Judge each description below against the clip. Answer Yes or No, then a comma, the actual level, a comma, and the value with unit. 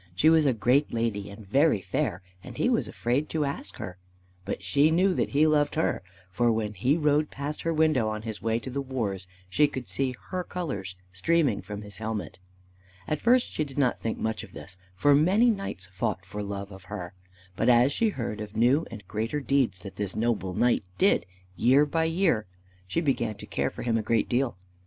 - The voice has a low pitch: Yes, low, 120 Hz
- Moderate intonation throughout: No, wide, 6.3 semitones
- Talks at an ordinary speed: No, fast, 210 wpm